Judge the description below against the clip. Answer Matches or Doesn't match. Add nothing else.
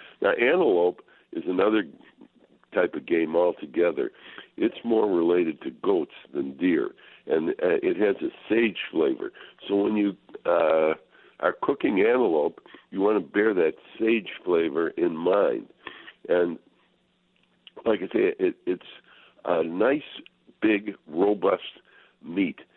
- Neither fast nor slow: Doesn't match